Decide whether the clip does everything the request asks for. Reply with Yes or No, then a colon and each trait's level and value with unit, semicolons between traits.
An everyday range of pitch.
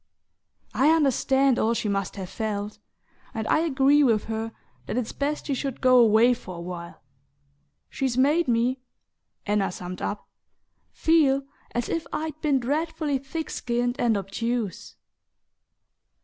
Yes: average, 4.5 semitones